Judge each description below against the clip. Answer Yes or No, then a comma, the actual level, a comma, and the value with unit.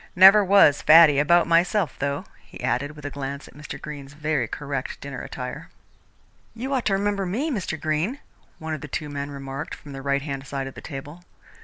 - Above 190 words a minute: Yes, average, 200 wpm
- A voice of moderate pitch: Yes, medium, 150 Hz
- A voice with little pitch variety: No, average, 4.0 semitones